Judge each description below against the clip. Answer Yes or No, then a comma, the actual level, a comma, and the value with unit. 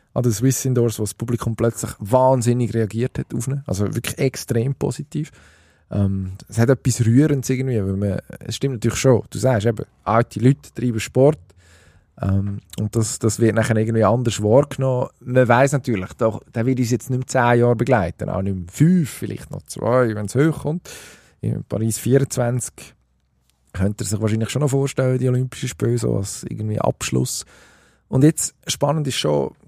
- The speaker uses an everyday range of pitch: Yes, average, 3.7 semitones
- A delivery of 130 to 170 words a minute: No, average, 180 wpm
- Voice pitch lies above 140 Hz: No, low, 120 Hz